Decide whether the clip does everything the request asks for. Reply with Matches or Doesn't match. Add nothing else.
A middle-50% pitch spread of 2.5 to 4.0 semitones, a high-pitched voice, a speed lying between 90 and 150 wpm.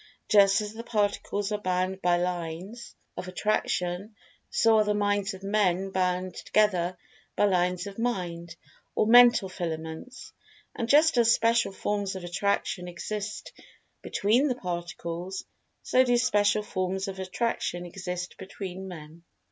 Matches